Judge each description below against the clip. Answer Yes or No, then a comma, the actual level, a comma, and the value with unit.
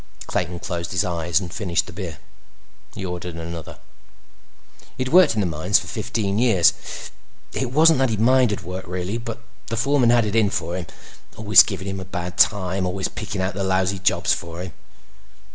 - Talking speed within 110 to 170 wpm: No, average, 185 wpm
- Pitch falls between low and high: No, very low, 95 Hz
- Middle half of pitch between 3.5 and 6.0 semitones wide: Yes, average, 3.9 semitones